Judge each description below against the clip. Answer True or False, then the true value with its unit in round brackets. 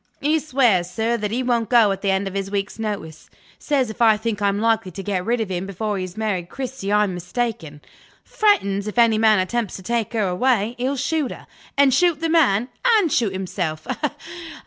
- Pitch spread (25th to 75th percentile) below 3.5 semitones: False (4.0 semitones)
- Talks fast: True (210 wpm)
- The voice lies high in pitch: True (220 Hz)